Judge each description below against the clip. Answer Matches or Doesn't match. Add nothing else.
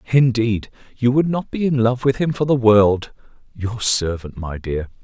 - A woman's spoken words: Doesn't match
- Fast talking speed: Doesn't match